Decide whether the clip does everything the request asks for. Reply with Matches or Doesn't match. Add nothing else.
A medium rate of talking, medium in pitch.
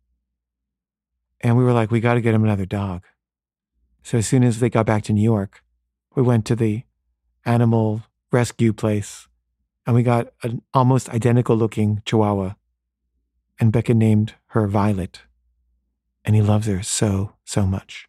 Doesn't match